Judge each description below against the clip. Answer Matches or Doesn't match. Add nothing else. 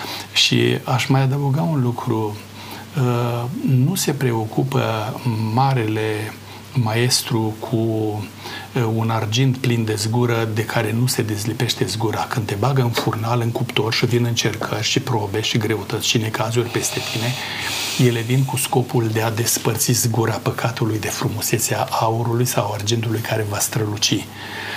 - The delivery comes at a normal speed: Matches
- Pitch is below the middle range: Matches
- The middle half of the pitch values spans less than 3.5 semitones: Matches